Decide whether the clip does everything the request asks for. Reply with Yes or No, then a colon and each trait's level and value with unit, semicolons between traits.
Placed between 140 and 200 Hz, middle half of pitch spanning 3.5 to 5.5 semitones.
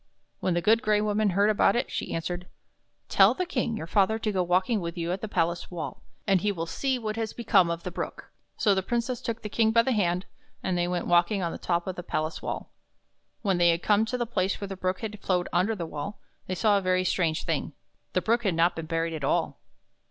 Yes: high, 190 Hz; average, 3.8 semitones